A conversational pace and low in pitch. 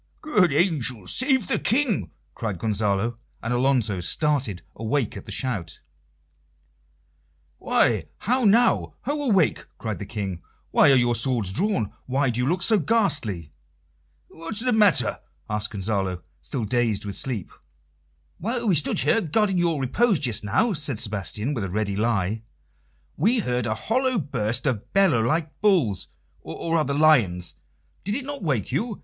Yes: average, 155 wpm; low, 130 Hz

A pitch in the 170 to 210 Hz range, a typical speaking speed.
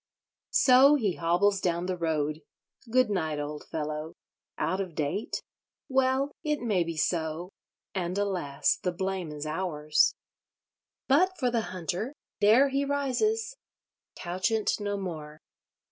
No: medium, 185 Hz; slow, 120 wpm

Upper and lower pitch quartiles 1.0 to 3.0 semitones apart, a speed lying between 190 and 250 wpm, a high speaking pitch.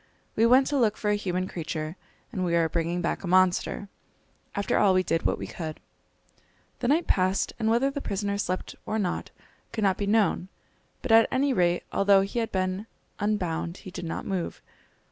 No: average, 3.6 semitones; average, 195 wpm; high, 195 Hz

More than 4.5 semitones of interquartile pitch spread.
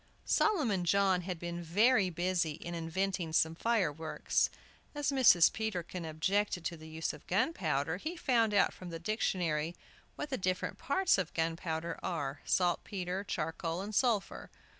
No: average, 4.0 semitones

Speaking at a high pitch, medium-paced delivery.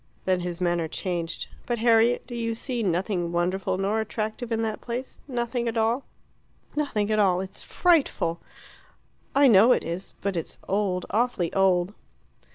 Yes: high, 210 Hz; average, 160 wpm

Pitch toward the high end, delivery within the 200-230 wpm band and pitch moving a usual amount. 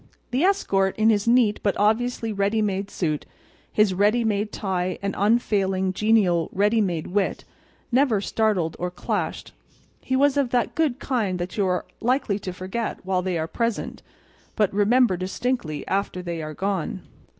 No: high, 205 Hz; average, 160 wpm; average, 3.8 semitones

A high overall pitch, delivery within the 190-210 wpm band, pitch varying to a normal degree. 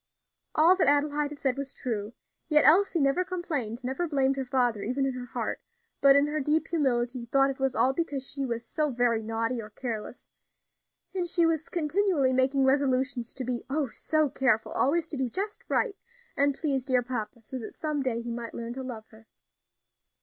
Yes: very high, 270 Hz; average, 195 wpm; average, 3.7 semitones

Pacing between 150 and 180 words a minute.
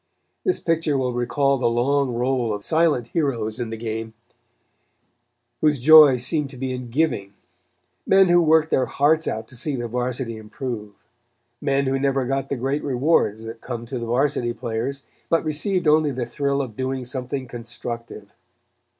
Yes: average, 165 wpm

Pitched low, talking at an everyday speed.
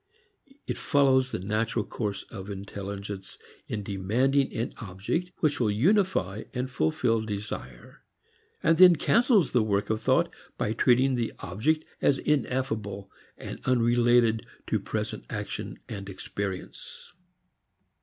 No: low, 115 Hz; slow, 125 wpm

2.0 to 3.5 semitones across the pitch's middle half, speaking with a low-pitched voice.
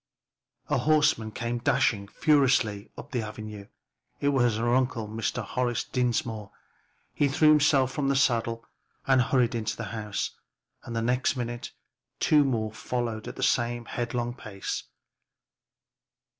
Yes: average, 3.0 semitones; low, 120 Hz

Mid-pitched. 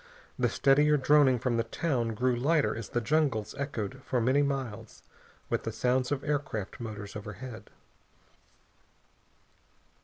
No: low, 125 Hz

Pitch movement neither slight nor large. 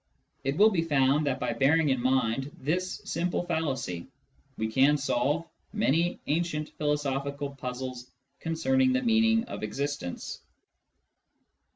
Yes: average, 4.2 semitones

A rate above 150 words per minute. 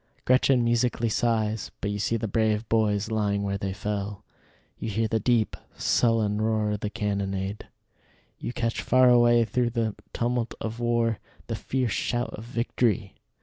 Yes: average, 160 wpm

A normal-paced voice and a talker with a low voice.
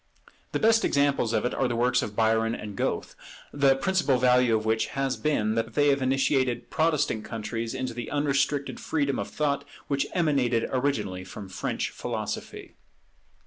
Yes: average, 165 wpm; low, 130 Hz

